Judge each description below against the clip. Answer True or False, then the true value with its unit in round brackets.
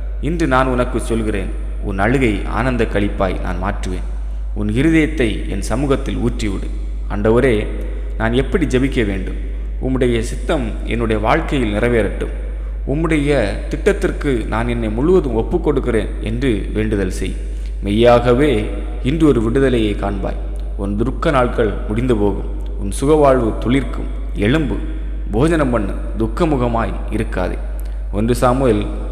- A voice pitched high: False (110 Hz)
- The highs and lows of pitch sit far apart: False (4.6 semitones)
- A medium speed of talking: True (110 wpm)